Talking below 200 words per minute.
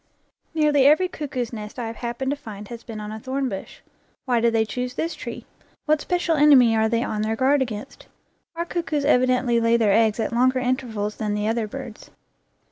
No: fast, 205 wpm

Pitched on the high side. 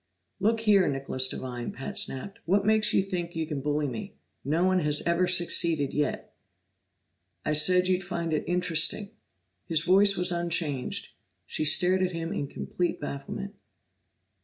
No: medium, 170 Hz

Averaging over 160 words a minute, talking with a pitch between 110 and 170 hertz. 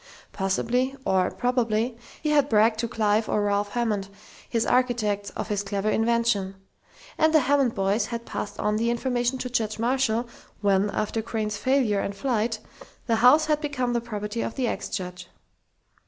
No: average, 170 wpm; high, 225 Hz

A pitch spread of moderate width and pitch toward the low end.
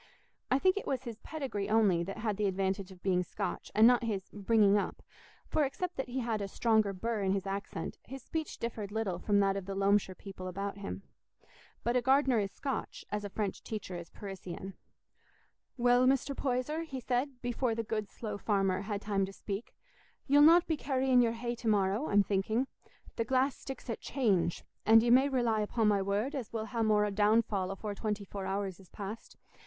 No: average, 3.9 semitones; high, 215 Hz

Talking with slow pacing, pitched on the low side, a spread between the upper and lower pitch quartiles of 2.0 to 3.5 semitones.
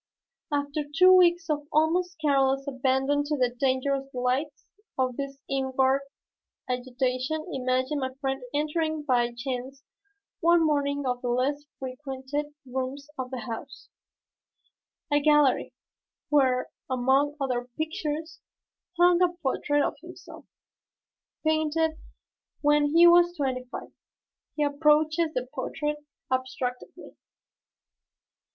No: slow, 115 wpm; very high, 280 Hz; average, 2.8 semitones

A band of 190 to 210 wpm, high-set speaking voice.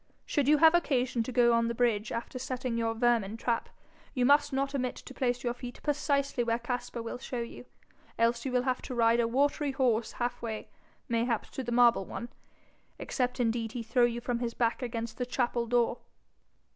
Yes: average, 200 wpm; high, 240 Hz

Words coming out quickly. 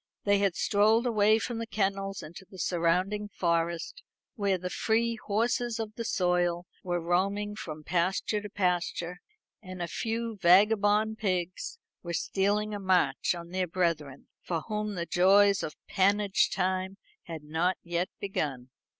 No: average, 150 wpm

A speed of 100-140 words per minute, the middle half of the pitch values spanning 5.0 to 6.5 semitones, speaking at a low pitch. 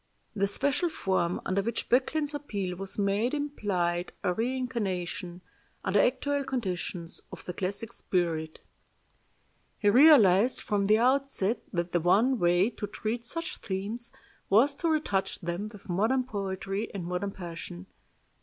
No: slow, 135 wpm; wide, 5.5 semitones; high, 200 Hz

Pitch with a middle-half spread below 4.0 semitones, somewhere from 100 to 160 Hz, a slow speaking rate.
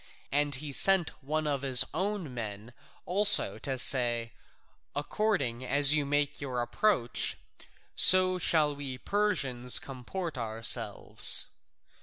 No: average, 5.3 semitones; medium, 140 Hz; slow, 115 wpm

